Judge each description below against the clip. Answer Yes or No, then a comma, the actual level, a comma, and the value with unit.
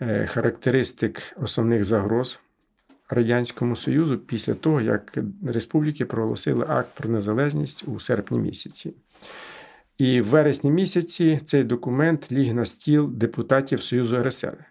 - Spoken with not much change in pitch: No, average, 4.0 semitones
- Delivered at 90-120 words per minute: Yes, average, 115 wpm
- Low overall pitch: Yes, low, 125 Hz